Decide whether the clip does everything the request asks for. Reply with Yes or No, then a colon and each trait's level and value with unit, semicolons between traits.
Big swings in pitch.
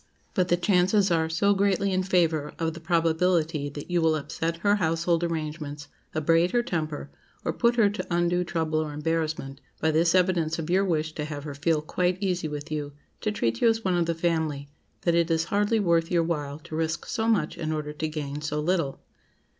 No: narrow, 2.6 semitones